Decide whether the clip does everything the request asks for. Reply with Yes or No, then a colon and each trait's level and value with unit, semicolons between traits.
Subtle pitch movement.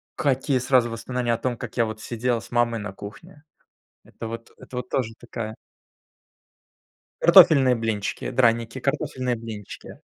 Yes: narrow, 2.2 semitones